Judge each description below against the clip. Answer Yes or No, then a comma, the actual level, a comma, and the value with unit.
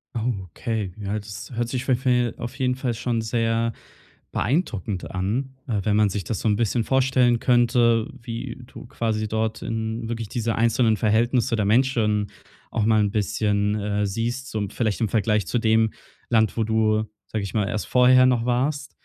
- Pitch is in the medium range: No, low, 115 Hz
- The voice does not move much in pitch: Yes, narrow, 2.3 semitones